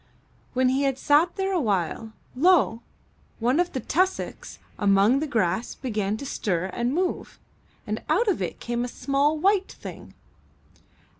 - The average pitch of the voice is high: Yes, very high, 260 Hz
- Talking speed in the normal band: Yes, average, 160 wpm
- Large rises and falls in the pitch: Yes, wide, 6.6 semitones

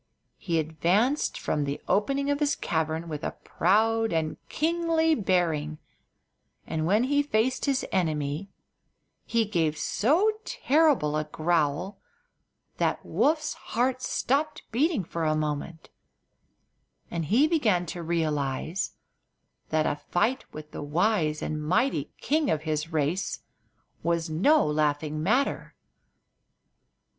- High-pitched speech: No, medium, 175 Hz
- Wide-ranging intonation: Yes, wide, 8.8 semitones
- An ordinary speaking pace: No, slow, 120 wpm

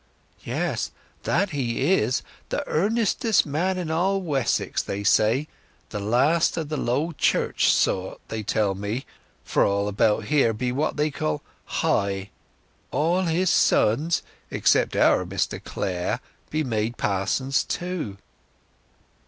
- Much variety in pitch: Yes, wide, 7.8 semitones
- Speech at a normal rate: No, slow, 120 wpm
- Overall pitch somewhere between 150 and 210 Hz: No, low, 135 Hz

